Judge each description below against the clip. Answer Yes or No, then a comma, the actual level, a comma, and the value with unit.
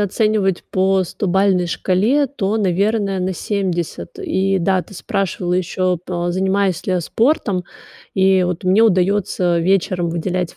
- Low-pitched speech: No, high, 190 Hz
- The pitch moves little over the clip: Yes, narrow, 1.9 semitones